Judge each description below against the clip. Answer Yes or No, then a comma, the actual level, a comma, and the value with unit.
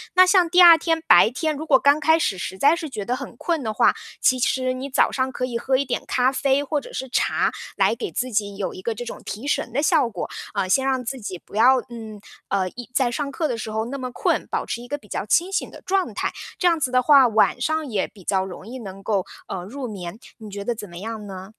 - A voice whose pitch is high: Yes, very high, 250 Hz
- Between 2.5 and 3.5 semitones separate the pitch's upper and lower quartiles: No, average, 5.2 semitones